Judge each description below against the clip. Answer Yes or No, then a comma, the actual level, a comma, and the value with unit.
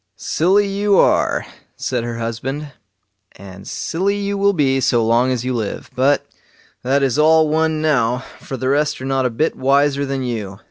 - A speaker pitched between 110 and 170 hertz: Yes, low, 135 Hz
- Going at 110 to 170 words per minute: No, average, 180 wpm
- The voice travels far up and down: No, average, 4.2 semitones